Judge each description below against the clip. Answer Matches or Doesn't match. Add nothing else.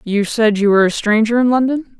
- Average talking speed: Doesn't match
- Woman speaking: Matches